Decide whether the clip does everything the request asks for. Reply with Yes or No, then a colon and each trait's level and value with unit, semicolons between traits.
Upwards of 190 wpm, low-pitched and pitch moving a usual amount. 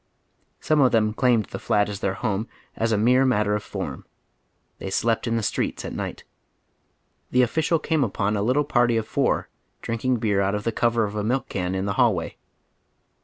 Yes: average, 200 wpm; low, 115 Hz; average, 3.3 semitones